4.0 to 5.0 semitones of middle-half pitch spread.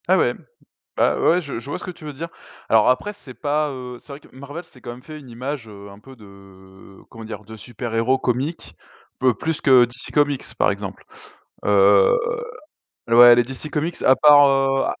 Yes: average, 4.5 semitones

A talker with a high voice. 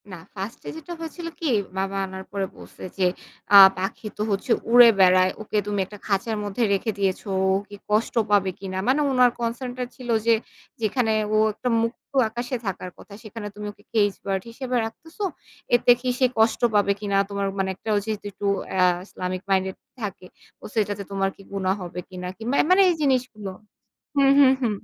Yes: high, 210 Hz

